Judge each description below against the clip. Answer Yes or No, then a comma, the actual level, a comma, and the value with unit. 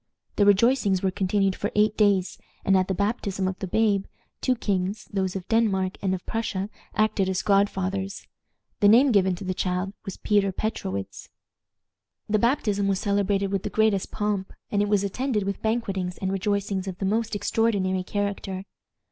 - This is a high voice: Yes, high, 200 Hz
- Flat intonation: Yes, narrow, 1.8 semitones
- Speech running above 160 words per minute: Yes, average, 175 wpm